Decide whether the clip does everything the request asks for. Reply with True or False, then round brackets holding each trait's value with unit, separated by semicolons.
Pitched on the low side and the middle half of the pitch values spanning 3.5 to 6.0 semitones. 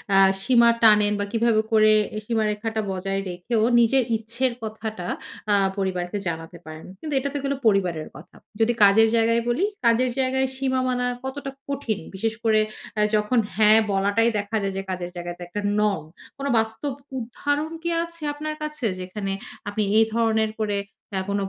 False (220 Hz; 3.9 semitones)